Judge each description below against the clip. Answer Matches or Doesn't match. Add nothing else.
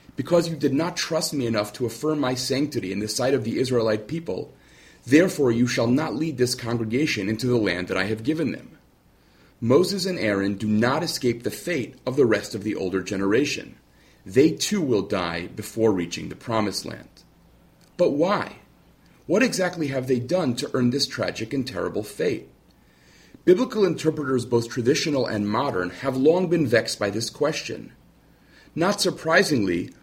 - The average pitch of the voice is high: Doesn't match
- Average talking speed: Matches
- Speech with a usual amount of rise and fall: Doesn't match